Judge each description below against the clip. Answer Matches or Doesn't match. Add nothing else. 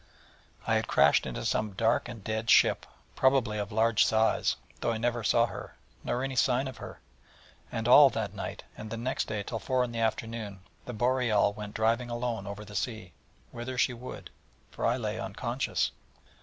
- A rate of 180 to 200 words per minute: Matches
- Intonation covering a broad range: Doesn't match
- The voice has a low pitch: Matches